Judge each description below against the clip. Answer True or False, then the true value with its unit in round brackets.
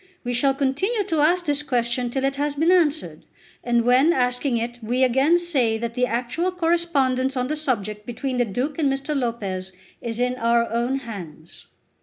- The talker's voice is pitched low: False (255 Hz)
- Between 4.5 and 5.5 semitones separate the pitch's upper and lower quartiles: False (3.8 semitones)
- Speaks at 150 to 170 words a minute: False (185 wpm)